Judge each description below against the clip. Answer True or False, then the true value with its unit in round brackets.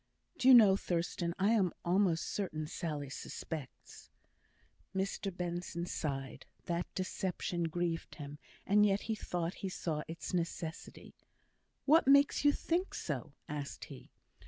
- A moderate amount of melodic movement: True (3.4 semitones)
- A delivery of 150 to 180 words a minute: False (135 wpm)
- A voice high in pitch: False (175 Hz)